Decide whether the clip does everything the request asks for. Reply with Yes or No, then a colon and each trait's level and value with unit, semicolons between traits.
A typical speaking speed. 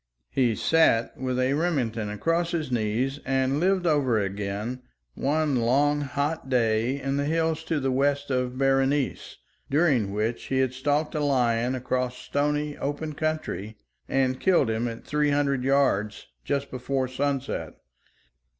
Yes: average, 145 wpm